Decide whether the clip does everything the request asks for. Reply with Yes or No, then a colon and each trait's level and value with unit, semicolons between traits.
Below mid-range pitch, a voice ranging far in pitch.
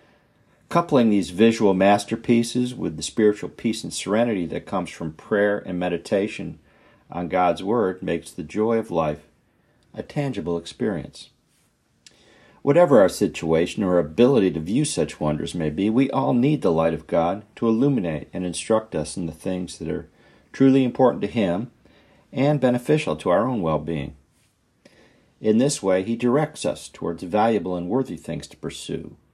Yes: low, 100 Hz; wide, 6.0 semitones